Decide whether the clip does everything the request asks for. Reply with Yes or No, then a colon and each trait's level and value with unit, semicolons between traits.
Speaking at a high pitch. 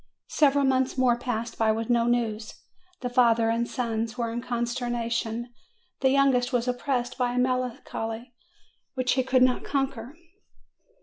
Yes: high, 245 Hz